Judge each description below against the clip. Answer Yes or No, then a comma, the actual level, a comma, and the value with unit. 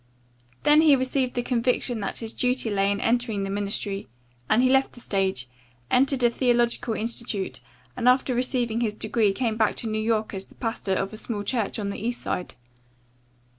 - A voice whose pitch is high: Yes, high, 230 Hz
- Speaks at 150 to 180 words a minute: No, average, 190 wpm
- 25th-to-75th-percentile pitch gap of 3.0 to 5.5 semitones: Yes, average, 3.3 semitones